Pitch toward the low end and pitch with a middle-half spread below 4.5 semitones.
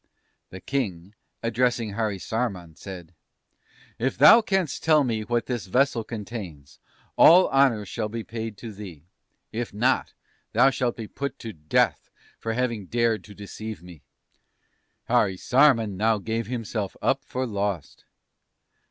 Yes: low, 115 Hz; average, 3.8 semitones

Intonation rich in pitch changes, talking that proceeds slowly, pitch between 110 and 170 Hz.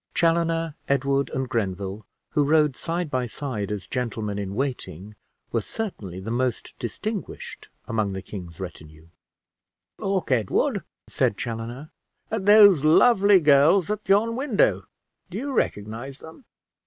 Yes: wide, 8.6 semitones; slow, 130 wpm; low, 135 Hz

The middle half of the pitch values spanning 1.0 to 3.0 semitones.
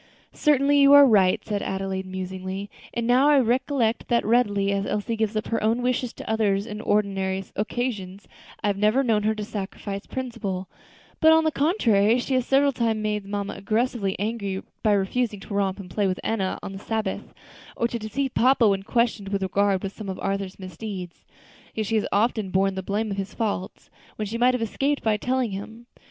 No: average, 3.4 semitones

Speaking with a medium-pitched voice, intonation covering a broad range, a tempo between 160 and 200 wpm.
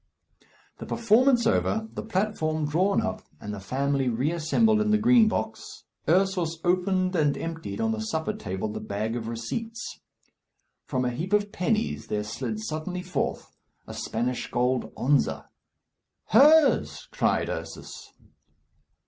No: medium, 180 Hz; wide, 8.7 semitones; slow, 135 wpm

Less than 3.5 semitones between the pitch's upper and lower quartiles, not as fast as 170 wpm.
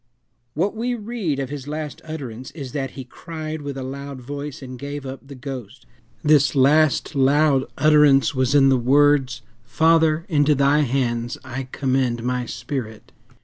Yes: narrow, 2.6 semitones; average, 160 wpm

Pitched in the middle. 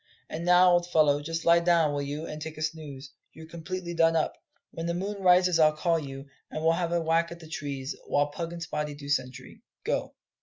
Yes: medium, 160 Hz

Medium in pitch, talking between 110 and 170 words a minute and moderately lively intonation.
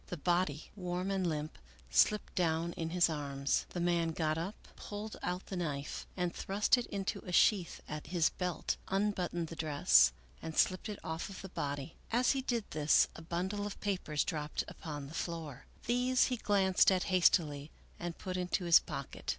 No: medium, 175 Hz; average, 185 wpm; average, 3.5 semitones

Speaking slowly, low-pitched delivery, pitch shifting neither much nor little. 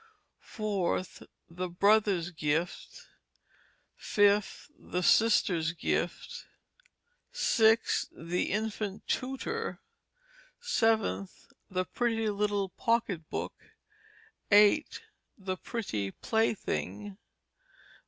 No: slow, 75 wpm; high, 200 Hz; average, 4.1 semitones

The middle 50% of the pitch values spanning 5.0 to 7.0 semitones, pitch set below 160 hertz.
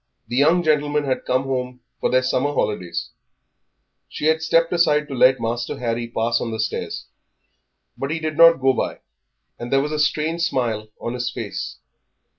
No: average, 4.2 semitones; low, 135 Hz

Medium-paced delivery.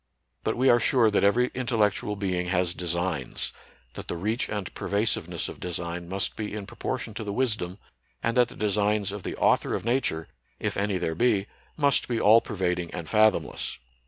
Yes: average, 185 wpm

